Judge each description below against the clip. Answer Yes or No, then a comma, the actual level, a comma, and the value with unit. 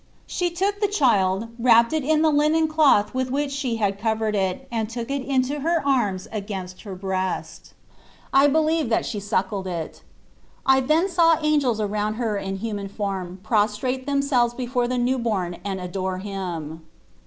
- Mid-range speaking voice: No, high, 230 Hz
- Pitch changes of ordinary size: No, wide, 6.0 semitones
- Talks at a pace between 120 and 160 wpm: No, average, 175 wpm